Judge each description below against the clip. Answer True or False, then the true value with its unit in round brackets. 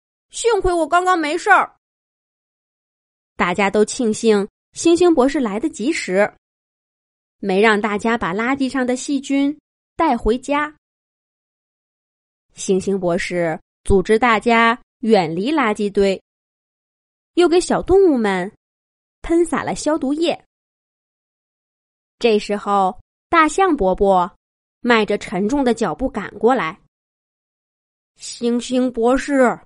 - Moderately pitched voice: False (235 Hz)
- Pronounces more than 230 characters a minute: False (165 characters per minute)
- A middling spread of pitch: False (6.2 semitones)